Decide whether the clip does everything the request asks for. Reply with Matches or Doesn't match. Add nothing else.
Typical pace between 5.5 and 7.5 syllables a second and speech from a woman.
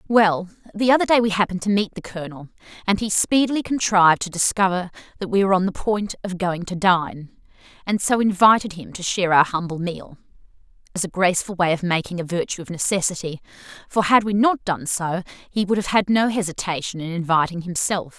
Matches